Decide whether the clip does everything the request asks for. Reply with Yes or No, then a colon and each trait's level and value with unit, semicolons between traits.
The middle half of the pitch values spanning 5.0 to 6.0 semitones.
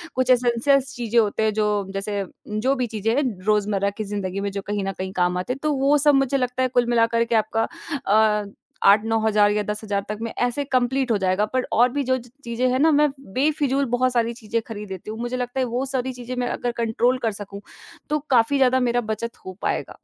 No: average, 3.4 semitones